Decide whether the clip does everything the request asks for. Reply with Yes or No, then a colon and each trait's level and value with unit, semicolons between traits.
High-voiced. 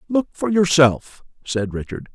No: medium, 150 Hz